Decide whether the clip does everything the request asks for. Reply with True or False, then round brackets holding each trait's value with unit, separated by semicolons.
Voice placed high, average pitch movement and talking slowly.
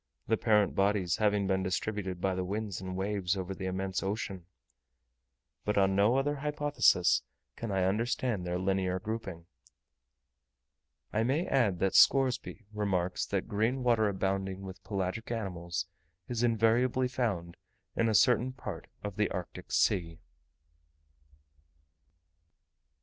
False (100 Hz; 3.4 semitones; 130 wpm)